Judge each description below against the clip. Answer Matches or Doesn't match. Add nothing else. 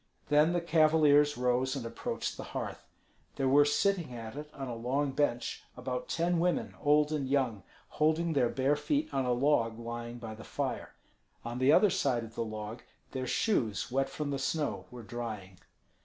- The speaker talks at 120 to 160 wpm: Doesn't match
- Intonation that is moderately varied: Matches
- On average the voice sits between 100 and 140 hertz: Matches